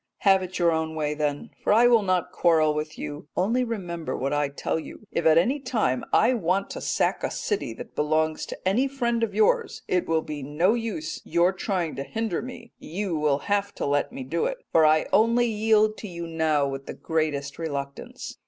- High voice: No, medium, 170 Hz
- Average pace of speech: No, fast, 210 wpm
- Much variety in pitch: Yes, wide, 6.3 semitones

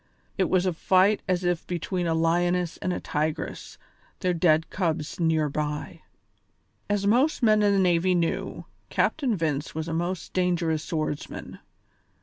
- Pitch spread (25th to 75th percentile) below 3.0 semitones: Yes, narrow, 2.5 semitones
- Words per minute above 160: No, average, 150 wpm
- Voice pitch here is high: No, medium, 175 Hz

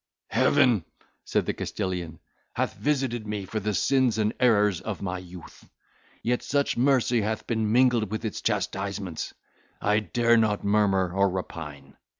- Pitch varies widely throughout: No, average, 3.8 semitones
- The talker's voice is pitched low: Yes, low, 105 Hz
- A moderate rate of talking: Yes, average, 150 wpm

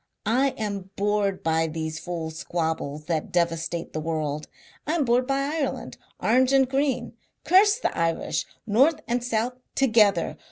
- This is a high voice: Yes, high, 205 Hz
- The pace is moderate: Yes, average, 150 wpm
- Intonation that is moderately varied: No, wide, 8.0 semitones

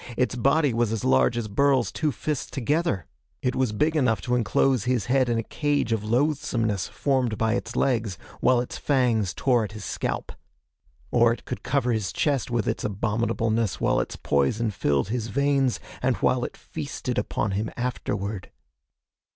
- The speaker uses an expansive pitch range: No, average, 3.6 semitones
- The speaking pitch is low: Yes, low, 120 Hz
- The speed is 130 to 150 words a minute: No, average, 175 wpm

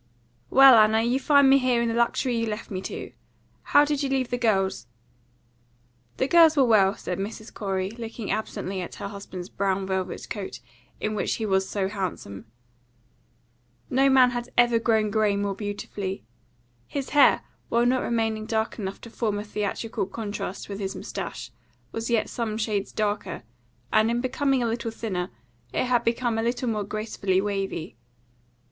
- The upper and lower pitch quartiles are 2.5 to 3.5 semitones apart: Yes, average, 3.2 semitones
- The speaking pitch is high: Yes, high, 220 Hz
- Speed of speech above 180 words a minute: No, average, 170 wpm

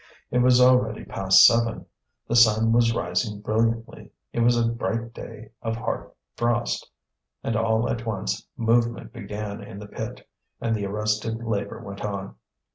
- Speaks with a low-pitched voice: Yes, low, 115 Hz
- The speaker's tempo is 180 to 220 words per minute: No, average, 155 wpm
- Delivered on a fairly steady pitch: Yes, narrow, 1.9 semitones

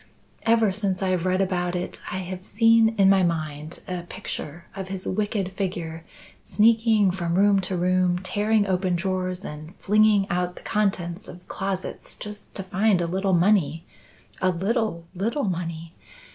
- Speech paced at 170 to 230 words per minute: No, average, 160 wpm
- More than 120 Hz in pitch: Yes, medium, 185 Hz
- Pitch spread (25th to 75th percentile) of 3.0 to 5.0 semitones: No, narrow, 2.4 semitones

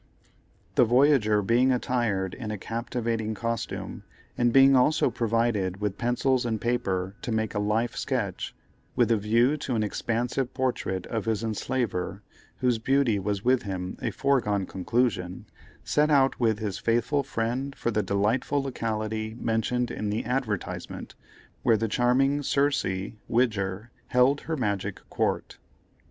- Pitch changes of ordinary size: Yes, average, 3.3 semitones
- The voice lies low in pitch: Yes, low, 115 Hz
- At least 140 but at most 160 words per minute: Yes, average, 145 wpm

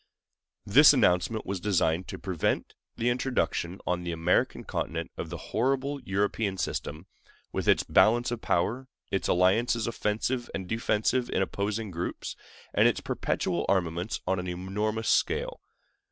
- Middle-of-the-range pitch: No, low, 100 Hz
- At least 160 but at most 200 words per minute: No, average, 140 wpm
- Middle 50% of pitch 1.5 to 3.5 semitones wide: No, average, 4.5 semitones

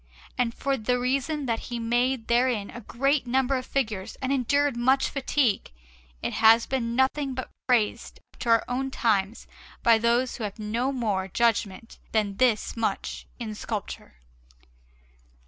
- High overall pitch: Yes, high, 240 Hz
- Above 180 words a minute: No, average, 160 wpm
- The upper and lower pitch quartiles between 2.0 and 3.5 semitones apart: Yes, average, 2.8 semitones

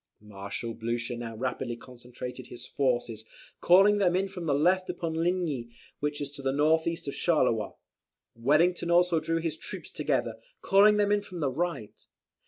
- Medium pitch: Yes, medium, 150 Hz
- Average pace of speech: Yes, average, 170 wpm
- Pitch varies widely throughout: Yes, wide, 6.2 semitones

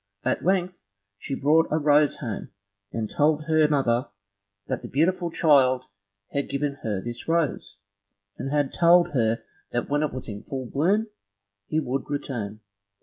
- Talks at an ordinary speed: Yes, average, 155 wpm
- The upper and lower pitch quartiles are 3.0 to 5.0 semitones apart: Yes, average, 4.1 semitones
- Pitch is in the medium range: Yes, medium, 145 Hz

